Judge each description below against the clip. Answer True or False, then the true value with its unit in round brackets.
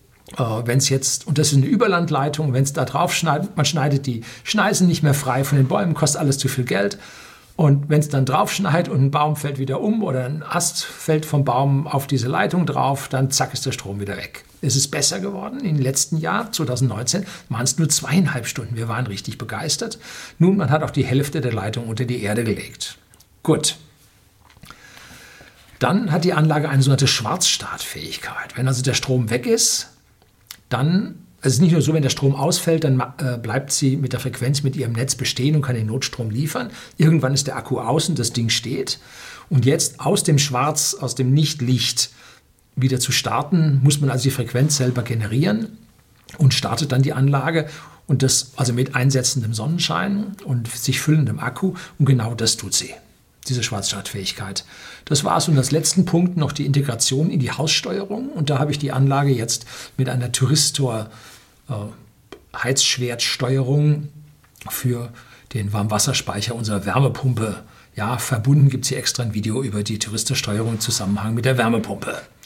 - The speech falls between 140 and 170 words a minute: False (180 wpm)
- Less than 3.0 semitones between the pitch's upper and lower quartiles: False (3.5 semitones)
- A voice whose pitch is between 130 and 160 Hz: True (135 Hz)